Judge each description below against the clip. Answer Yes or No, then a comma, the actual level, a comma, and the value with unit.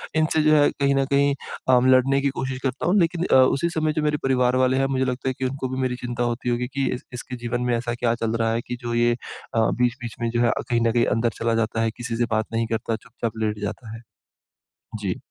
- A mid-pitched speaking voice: No, low, 125 Hz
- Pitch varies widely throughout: No, narrow, 2.4 semitones